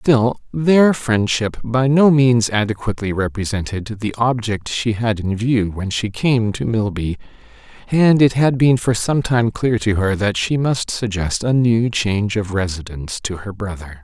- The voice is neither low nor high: No, low, 110 Hz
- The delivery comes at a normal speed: Yes, average, 175 wpm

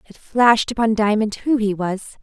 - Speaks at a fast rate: No, average, 190 wpm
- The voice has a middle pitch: No, high, 215 Hz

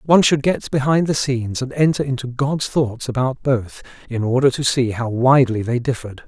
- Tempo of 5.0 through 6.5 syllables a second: Yes, 5.5 syllables/s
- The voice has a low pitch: Yes, low, 130 Hz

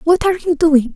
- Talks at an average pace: No, fast, 250 wpm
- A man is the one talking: No, female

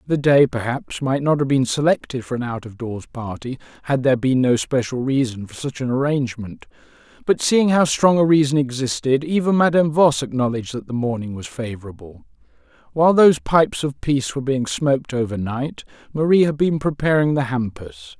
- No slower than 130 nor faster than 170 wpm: No, average, 185 wpm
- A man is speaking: Yes, male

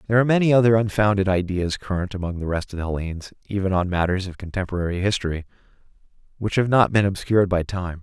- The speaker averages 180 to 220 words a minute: Yes, average, 195 wpm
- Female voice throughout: No, male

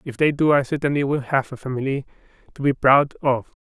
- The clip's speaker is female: No, male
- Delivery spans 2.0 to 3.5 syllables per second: No, 5.9 syllables/s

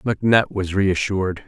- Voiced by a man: Yes, male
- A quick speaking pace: No, slow, 120 wpm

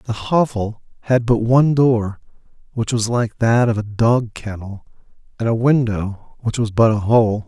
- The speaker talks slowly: No, average, 175 wpm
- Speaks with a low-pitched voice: Yes, low, 115 Hz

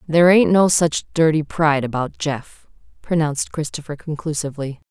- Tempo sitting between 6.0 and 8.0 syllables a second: No, 5.4 syllables/s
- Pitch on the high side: No, medium, 155 Hz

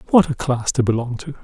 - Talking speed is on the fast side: Yes, fast, 250 wpm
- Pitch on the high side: No, low, 130 Hz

